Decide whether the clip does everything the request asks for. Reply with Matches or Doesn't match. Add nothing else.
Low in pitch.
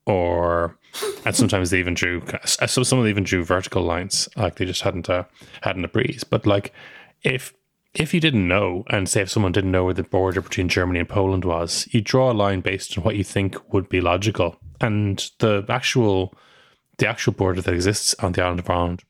Matches